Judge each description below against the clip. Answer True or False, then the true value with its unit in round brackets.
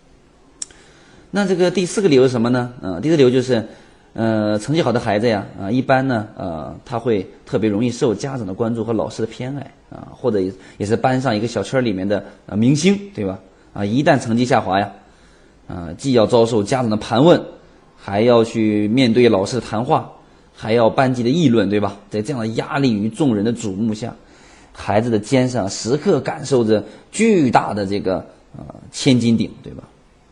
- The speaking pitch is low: True (115 Hz)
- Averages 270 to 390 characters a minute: True (290 characters per minute)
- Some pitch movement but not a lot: True (3.7 semitones)